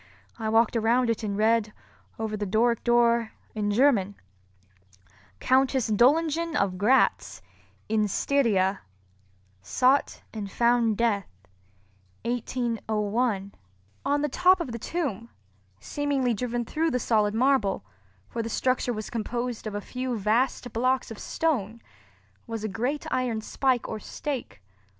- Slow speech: Yes, slow, 125 wpm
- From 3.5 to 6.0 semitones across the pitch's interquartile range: Yes, average, 3.8 semitones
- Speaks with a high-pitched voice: Yes, high, 230 Hz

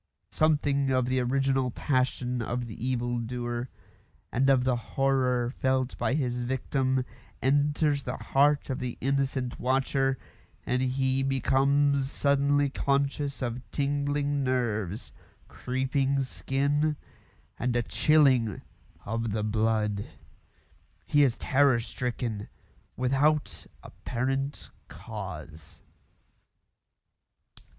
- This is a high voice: No, low, 130 Hz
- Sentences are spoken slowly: Yes, slow, 100 wpm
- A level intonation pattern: Yes, narrow, 2.3 semitones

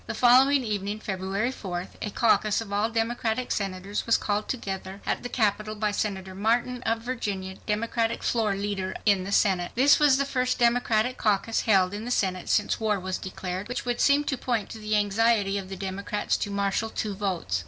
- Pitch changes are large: No, average, 3.0 semitones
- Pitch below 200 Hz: No, high, 210 Hz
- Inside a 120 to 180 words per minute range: No, average, 195 wpm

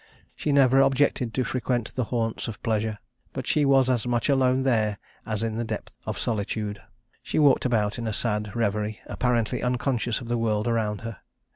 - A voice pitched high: No, low, 115 Hz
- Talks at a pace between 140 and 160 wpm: No, average, 185 wpm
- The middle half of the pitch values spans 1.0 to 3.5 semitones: Yes, average, 2.9 semitones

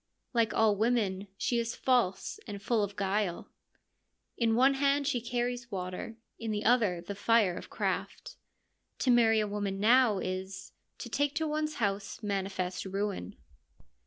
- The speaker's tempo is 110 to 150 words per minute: No, average, 160 wpm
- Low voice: No, high, 215 Hz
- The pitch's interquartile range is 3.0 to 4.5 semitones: Yes, average, 3.6 semitones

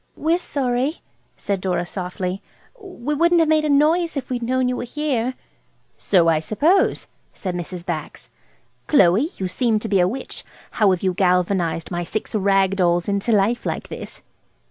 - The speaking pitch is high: Yes, high, 210 Hz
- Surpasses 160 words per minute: Yes, average, 170 wpm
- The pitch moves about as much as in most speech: No, wide, 7.3 semitones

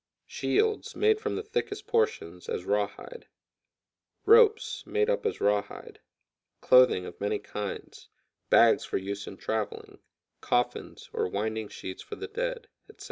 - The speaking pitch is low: No, very high, 425 Hz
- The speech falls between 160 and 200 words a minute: No, slow, 135 wpm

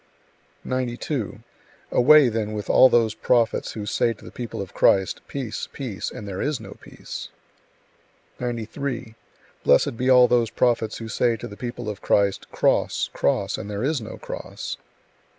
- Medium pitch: No, low, 115 Hz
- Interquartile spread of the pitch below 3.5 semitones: Yes, average, 2.9 semitones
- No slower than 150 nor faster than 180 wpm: Yes, average, 160 wpm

